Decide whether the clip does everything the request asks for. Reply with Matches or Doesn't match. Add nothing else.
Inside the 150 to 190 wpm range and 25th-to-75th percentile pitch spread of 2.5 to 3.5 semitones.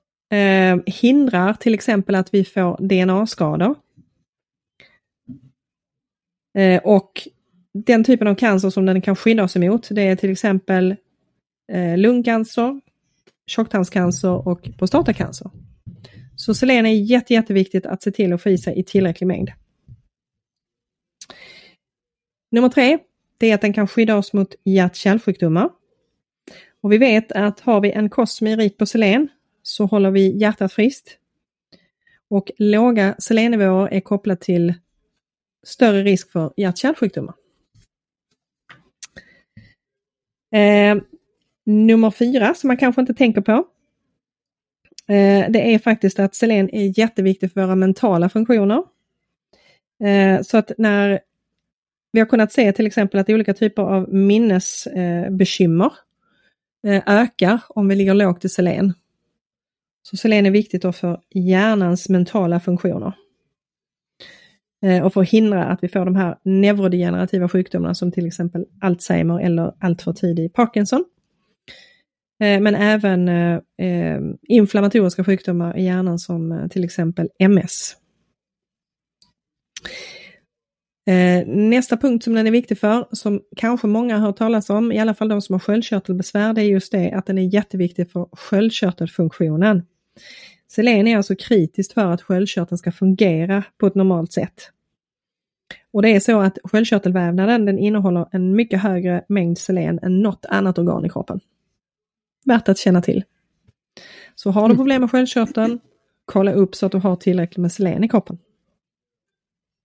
Doesn't match